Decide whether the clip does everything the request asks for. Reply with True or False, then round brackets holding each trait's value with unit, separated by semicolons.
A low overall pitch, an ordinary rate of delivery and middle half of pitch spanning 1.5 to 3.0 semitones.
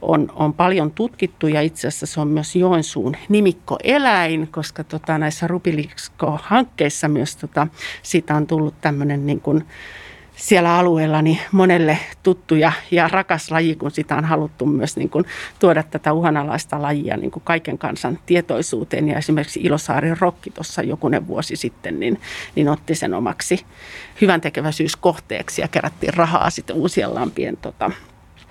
False (160 Hz; 140 wpm; 2.5 semitones)